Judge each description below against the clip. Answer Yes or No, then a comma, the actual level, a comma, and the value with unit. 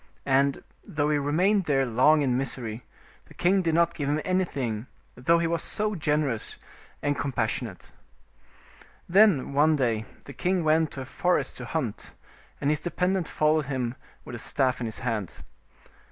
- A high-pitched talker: No, medium, 145 Hz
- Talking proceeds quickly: No, average, 165 wpm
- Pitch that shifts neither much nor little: Yes, average, 4.4 semitones